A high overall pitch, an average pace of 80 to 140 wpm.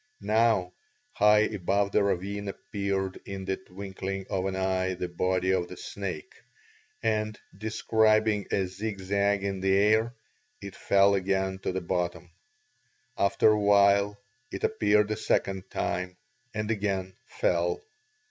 No: low, 100 Hz; slow, 135 wpm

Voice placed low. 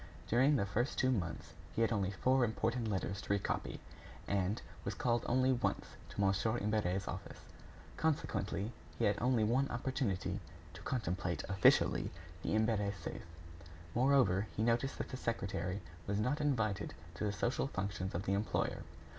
Yes: low, 110 Hz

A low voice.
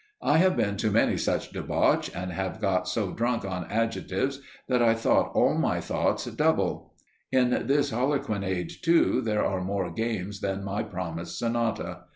Yes: low, 105 Hz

